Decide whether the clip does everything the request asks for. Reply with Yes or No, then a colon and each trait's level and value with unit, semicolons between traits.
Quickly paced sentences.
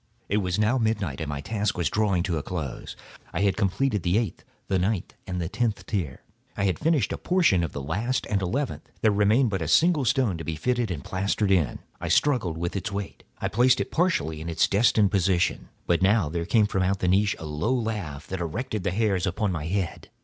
Yes: fast, 230 wpm